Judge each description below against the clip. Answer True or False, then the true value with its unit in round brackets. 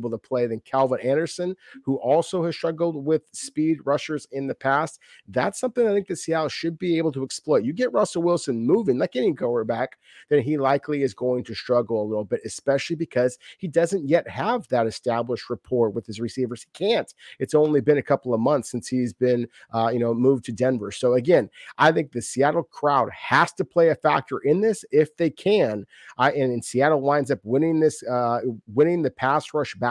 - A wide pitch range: False (4.8 semitones)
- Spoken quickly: True (215 wpm)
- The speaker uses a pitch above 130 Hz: True (140 Hz)